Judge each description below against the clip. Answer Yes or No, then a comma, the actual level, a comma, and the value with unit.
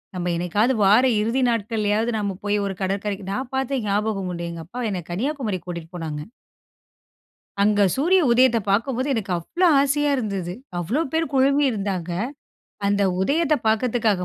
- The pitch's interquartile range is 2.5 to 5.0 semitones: No, wide, 5.4 semitones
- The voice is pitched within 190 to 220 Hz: Yes, high, 210 Hz